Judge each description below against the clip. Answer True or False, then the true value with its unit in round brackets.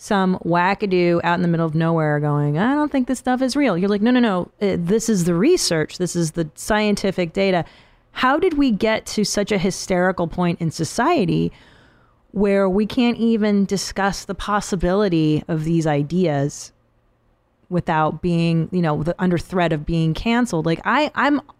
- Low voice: False (180 Hz)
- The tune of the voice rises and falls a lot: False (4.3 semitones)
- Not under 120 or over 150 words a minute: False (180 wpm)